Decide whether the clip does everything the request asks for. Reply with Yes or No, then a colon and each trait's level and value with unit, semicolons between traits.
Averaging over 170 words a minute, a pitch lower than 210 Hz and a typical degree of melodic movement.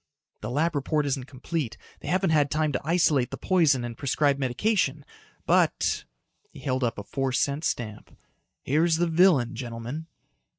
No: average, 160 wpm; medium, 140 Hz; average, 4.1 semitones